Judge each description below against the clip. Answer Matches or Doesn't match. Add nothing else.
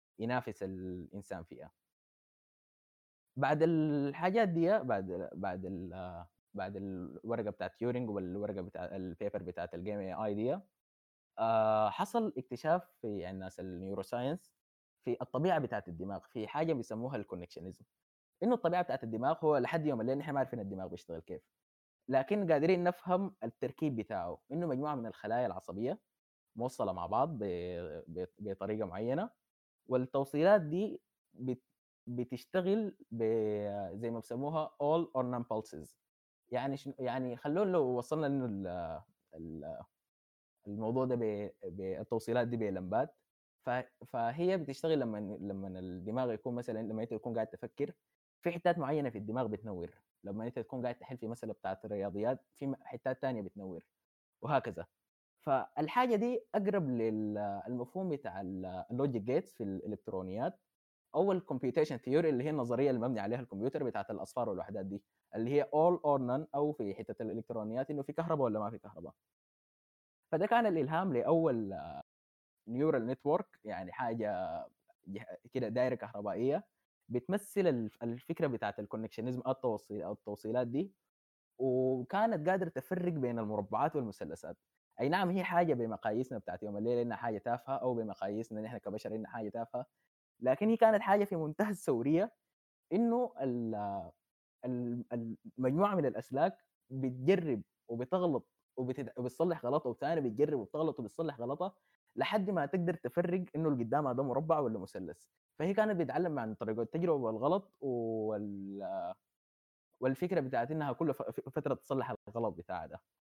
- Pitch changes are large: Matches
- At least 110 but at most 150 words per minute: Matches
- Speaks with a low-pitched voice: Matches